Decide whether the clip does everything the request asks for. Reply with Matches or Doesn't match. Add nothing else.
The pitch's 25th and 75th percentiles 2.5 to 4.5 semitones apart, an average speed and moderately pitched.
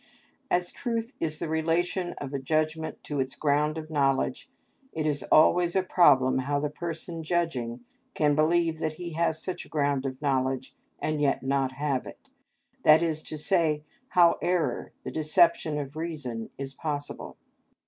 Matches